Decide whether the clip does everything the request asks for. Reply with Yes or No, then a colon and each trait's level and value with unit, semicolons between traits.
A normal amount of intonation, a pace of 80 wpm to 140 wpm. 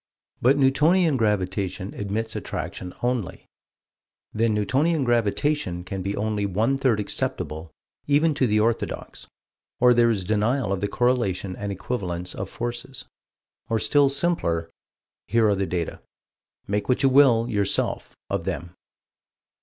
Yes: average, 4.7 semitones; slow, 135 wpm